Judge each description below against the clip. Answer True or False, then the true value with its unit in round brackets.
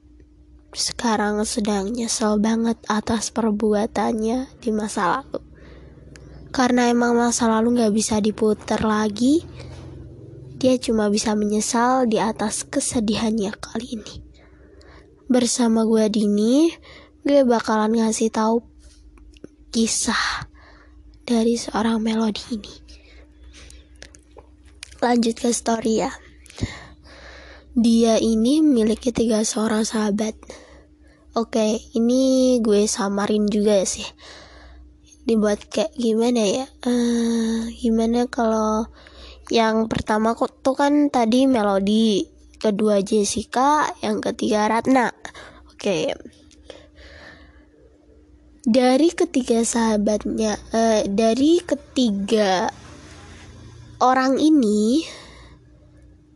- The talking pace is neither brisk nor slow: False (85 wpm)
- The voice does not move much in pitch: True (2.2 semitones)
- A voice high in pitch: True (225 Hz)